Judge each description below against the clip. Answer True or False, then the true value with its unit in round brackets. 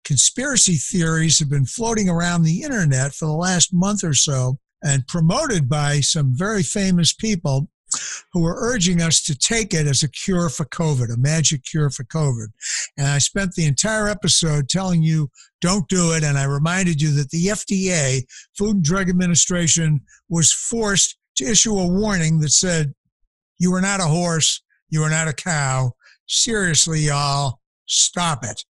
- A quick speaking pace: False (170 wpm)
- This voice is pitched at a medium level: True (165 Hz)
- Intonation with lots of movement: False (4.2 semitones)